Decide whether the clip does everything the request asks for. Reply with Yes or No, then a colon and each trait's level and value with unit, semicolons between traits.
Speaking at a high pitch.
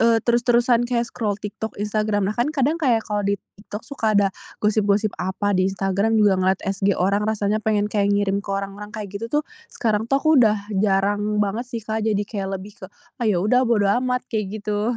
Yes: high, 210 Hz